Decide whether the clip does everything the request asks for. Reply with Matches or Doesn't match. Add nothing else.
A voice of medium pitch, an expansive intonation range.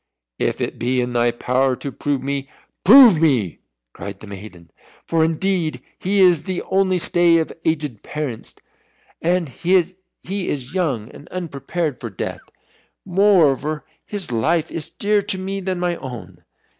Matches